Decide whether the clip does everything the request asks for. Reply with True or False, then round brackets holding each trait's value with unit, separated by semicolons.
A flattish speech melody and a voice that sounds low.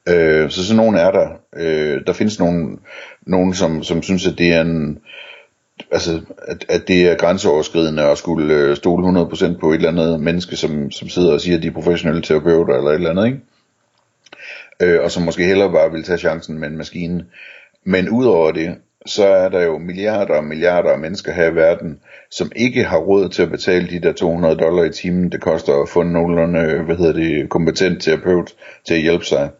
True (1.7 semitones; 85 Hz)